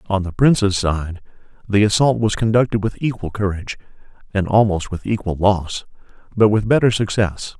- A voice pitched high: No, low, 100 Hz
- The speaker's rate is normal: Yes, average, 160 wpm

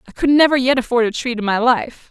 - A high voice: Yes, high, 240 Hz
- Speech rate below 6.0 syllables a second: No, 6.2 syllables/s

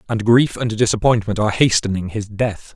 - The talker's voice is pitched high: No, low, 110 Hz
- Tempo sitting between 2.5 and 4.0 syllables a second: No, 5.5 syllables/s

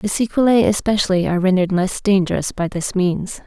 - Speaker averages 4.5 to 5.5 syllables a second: No, 5.9 syllables/s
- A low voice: No, high, 190 Hz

